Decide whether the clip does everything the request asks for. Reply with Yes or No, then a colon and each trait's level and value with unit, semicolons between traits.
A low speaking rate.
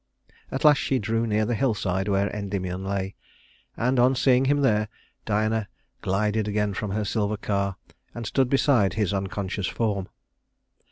No: average, 155 wpm